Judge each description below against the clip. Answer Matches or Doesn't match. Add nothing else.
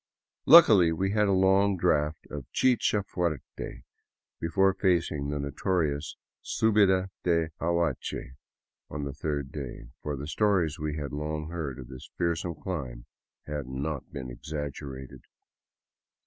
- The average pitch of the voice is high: Doesn't match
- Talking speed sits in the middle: Doesn't match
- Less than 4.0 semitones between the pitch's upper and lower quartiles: Doesn't match